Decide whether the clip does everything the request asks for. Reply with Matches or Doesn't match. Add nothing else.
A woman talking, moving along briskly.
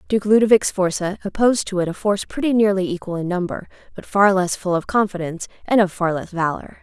Matches